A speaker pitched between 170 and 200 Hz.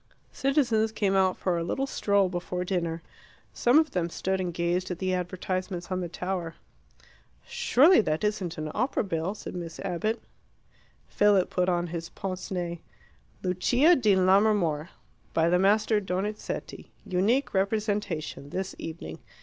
Yes: medium, 185 Hz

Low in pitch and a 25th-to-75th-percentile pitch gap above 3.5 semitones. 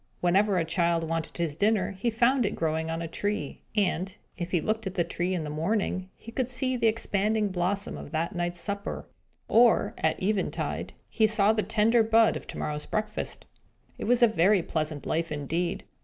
No: high, 190 Hz; average, 4.5 semitones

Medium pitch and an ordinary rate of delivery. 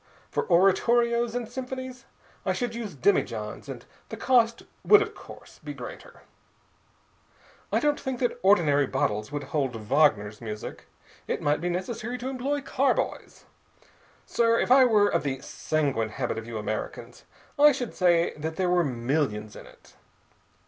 Yes: medium, 180 Hz; average, 155 wpm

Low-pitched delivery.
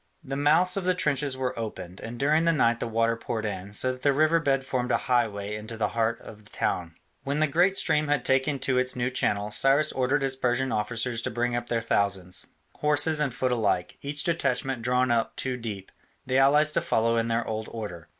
Yes: low, 125 Hz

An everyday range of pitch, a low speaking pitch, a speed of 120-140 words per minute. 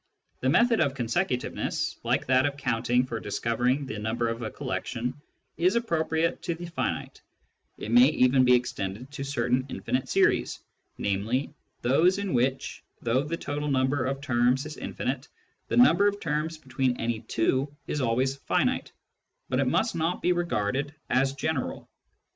No: average, 3.9 semitones; low, 130 Hz; average, 160 wpm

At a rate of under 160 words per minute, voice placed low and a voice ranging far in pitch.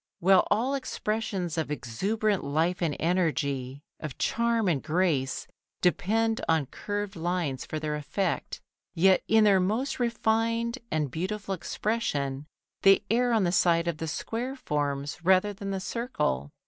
No: average, 145 wpm; medium, 185 Hz; wide, 6.2 semitones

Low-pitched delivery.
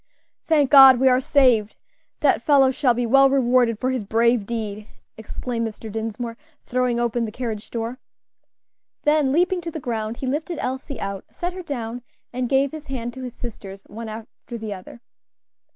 No: high, 245 Hz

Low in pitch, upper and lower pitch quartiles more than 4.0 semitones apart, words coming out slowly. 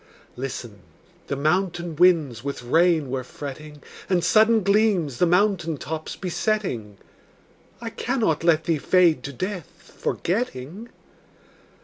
No: medium, 165 Hz; wide, 5.4 semitones; slow, 115 wpm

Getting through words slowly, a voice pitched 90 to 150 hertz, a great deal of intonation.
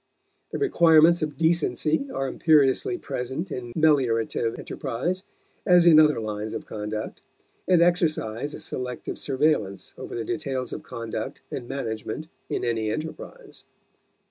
Yes: slow, 130 wpm; medium, 140 Hz; wide, 5.8 semitones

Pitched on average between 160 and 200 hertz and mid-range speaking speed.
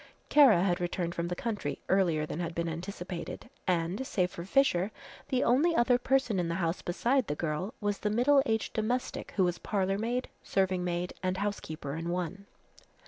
Yes: high, 190 Hz; average, 185 wpm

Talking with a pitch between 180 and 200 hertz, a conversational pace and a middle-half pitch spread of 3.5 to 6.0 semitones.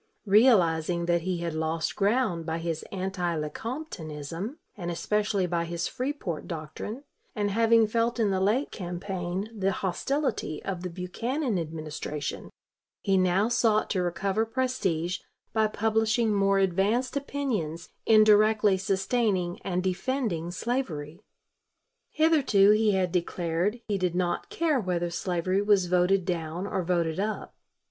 No: high, 190 Hz; slow, 130 wpm; average, 4.2 semitones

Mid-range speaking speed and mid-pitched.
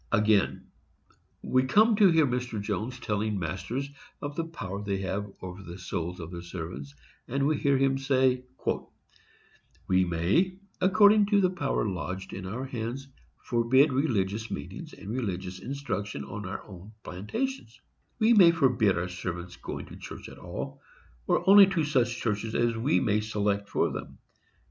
No: average, 160 wpm; low, 115 Hz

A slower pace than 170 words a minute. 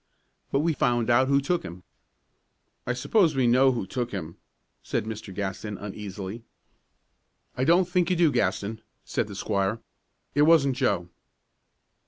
Yes: average, 150 wpm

